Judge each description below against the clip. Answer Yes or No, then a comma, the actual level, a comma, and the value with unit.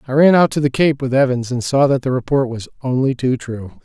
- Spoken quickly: Yes, fast, 265 wpm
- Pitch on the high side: No, low, 130 Hz